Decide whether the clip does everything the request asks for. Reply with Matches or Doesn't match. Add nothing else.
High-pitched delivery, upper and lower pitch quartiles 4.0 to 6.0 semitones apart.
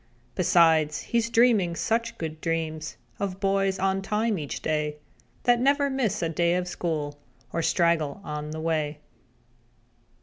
Doesn't match